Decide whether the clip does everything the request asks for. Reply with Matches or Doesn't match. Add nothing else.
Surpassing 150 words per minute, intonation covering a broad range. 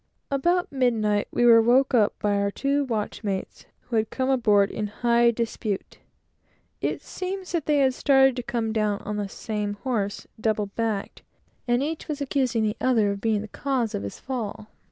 Doesn't match